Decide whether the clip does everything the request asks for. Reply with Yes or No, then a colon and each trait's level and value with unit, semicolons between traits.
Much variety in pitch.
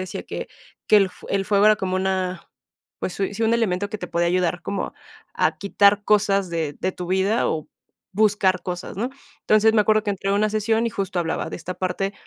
No: narrow, 2.4 semitones